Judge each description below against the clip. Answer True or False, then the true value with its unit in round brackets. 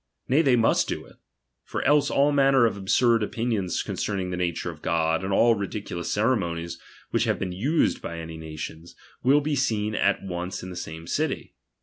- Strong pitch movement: True (6.1 semitones)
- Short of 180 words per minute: False (195 wpm)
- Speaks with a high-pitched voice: False (100 Hz)